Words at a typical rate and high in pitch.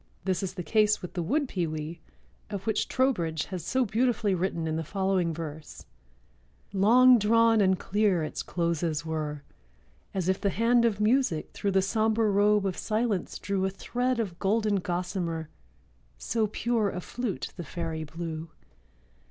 Yes: average, 160 wpm; high, 195 Hz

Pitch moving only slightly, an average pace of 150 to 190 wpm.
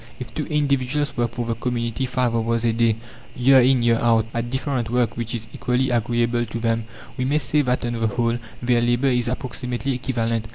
No: narrow, 1.6 semitones; fast, 205 wpm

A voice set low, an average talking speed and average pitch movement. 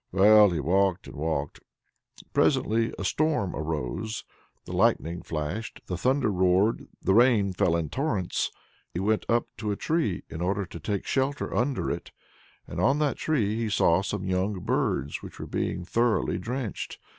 Yes: low, 100 Hz; average, 165 wpm; average, 4.7 semitones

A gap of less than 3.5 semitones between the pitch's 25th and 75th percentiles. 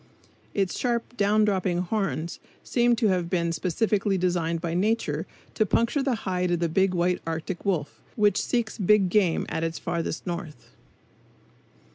No: average, 3.8 semitones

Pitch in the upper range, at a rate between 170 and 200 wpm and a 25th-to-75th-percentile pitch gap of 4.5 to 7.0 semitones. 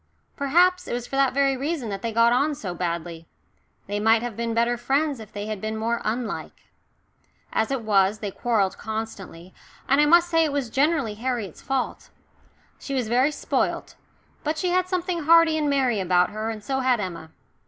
Yes: high, 240 Hz; average, 195 wpm; average, 5.0 semitones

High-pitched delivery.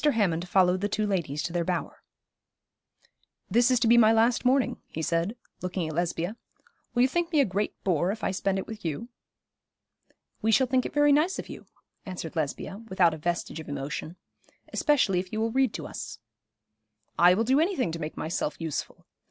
Yes: high, 195 Hz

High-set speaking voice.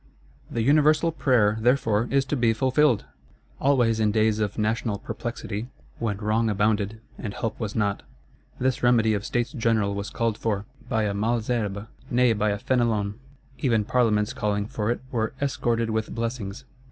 No: low, 110 Hz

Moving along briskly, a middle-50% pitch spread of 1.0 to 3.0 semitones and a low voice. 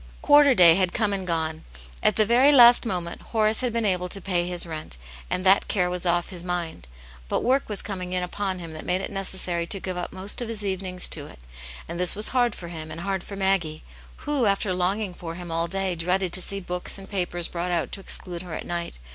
No: fast, 240 wpm; narrow, 2.4 semitones; medium, 185 Hz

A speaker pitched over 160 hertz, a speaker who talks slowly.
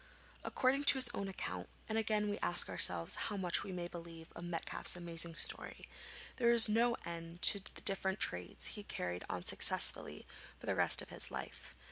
No: medium, 185 Hz; average, 185 wpm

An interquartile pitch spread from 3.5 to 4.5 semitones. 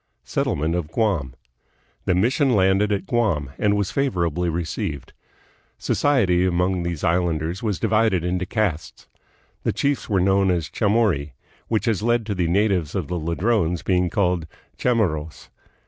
Yes: average, 4.1 semitones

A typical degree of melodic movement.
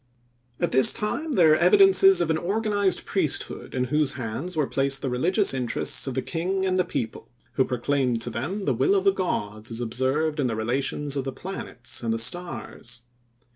No: wide, 6.8 semitones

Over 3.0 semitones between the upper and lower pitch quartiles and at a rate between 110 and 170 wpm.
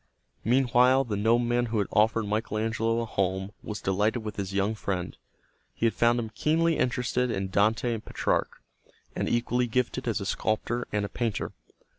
No: average, 2.7 semitones; average, 165 wpm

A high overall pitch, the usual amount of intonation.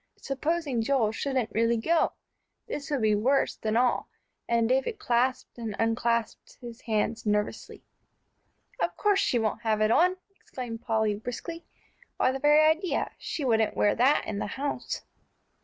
Yes: high, 240 Hz; average, 4.0 semitones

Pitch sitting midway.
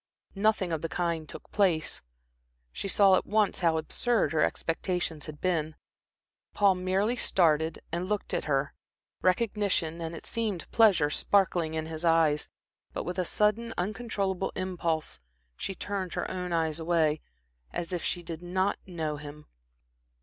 Yes: medium, 175 Hz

